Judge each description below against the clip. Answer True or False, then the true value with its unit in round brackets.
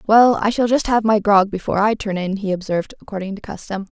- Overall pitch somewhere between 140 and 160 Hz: False (205 Hz)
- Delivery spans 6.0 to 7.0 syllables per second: True (6.3 syllables/s)